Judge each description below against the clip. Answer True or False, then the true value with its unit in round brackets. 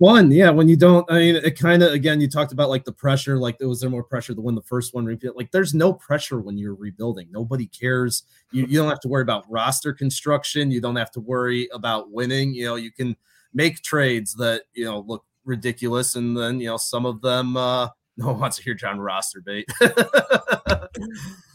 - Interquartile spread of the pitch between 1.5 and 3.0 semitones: False (3.7 semitones)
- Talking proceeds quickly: True (220 wpm)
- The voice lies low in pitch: True (125 Hz)